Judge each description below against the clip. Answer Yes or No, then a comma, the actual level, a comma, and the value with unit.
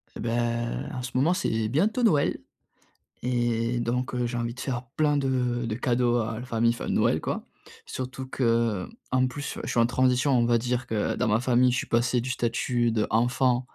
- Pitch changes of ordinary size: No, narrow, 1.6 semitones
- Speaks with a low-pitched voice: Yes, low, 125 Hz